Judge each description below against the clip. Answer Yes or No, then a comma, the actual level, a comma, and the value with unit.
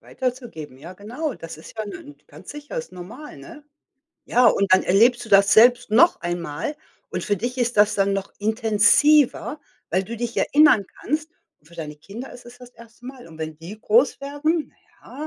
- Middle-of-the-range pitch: No, high, 225 Hz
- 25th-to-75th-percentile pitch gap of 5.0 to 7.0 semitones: Yes, wide, 5.5 semitones